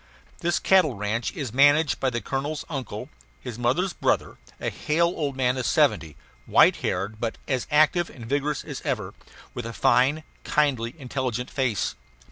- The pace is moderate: Yes, average, 160 wpm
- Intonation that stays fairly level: No, average, 4.0 semitones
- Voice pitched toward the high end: No, low, 130 Hz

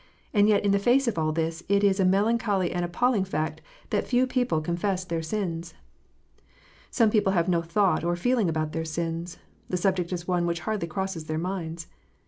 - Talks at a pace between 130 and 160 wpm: No, average, 195 wpm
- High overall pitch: No, medium, 180 Hz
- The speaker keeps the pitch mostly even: No, average, 3.4 semitones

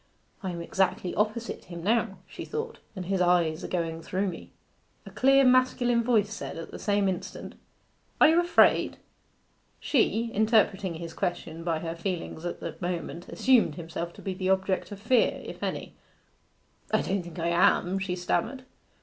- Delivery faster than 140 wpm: Yes, average, 170 wpm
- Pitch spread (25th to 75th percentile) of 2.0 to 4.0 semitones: No, average, 4.6 semitones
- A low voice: No, high, 190 Hz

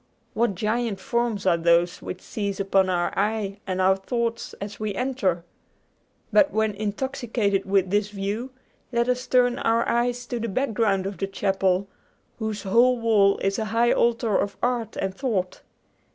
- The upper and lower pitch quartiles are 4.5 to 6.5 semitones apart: No, average, 3.4 semitones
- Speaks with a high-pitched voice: Yes, high, 210 Hz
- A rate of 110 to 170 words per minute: Yes, average, 165 wpm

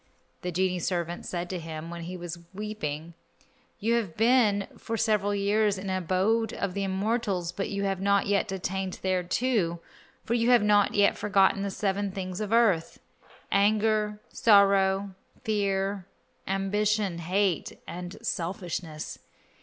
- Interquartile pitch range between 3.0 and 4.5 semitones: No, narrow, 2.5 semitones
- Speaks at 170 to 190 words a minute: No, average, 145 wpm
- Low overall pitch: No, high, 195 Hz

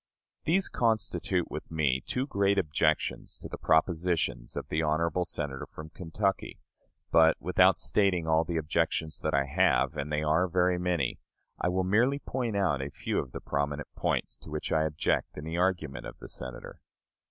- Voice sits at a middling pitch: No, very low, 80 Hz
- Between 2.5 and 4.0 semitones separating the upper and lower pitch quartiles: Yes, average, 3.4 semitones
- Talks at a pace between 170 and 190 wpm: Yes, average, 175 wpm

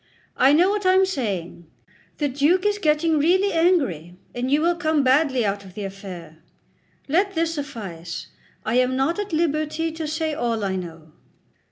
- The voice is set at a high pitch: Yes, very high, 290 Hz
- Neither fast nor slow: Yes, average, 175 wpm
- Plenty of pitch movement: Yes, wide, 8.5 semitones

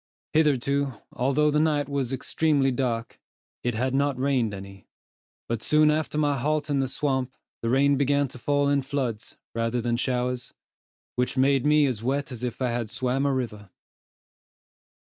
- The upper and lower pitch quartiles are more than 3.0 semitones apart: No, average, 2.7 semitones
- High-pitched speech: No, low, 135 Hz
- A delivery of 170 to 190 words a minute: Yes, average, 175 wpm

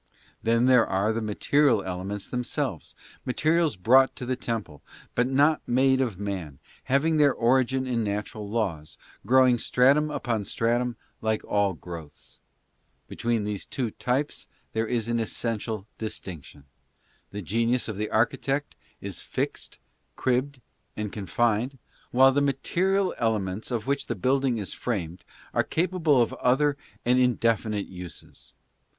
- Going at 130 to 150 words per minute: Yes, average, 145 wpm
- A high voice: No, low, 120 Hz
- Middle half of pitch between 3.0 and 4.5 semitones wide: Yes, average, 4.2 semitones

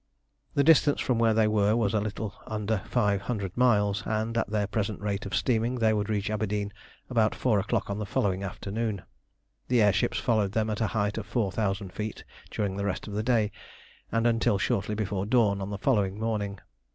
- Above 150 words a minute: Yes, fast, 205 wpm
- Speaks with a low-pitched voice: Yes, low, 105 Hz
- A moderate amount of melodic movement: No, narrow, 2.0 semitones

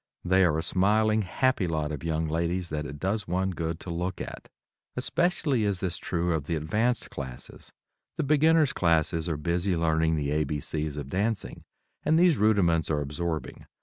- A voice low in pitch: Yes, very low, 85 Hz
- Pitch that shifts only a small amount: No, average, 4.5 semitones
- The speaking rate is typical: Yes, average, 180 wpm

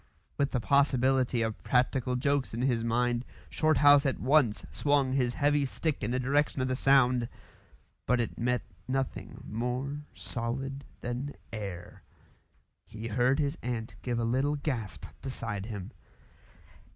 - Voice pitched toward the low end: Yes, low, 125 Hz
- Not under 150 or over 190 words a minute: No, average, 140 wpm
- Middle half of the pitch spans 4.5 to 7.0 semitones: No, average, 2.9 semitones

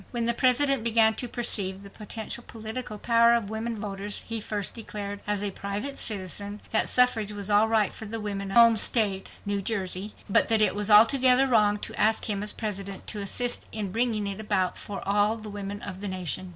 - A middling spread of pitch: No, narrow, 2.2 semitones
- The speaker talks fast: Yes, fast, 210 wpm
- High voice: Yes, high, 210 Hz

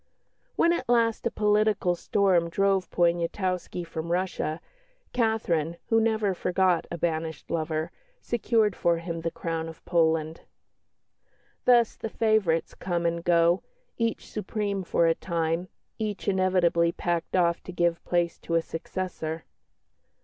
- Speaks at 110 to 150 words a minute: Yes, slow, 135 wpm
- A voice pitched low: No, medium, 175 Hz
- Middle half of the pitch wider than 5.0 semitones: No, average, 3.5 semitones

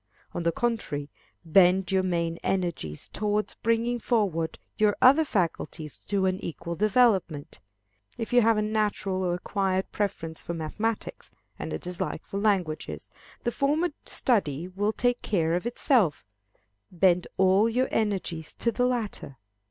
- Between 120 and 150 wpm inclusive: Yes, average, 145 wpm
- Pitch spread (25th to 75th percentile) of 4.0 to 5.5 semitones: Yes, average, 4.7 semitones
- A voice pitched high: Yes, high, 195 Hz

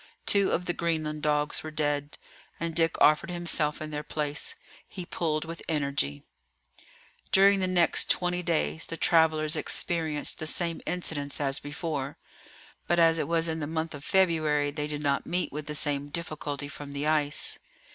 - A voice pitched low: No, medium, 155 Hz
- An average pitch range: No, narrow, 2.3 semitones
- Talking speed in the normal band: Yes, average, 170 wpm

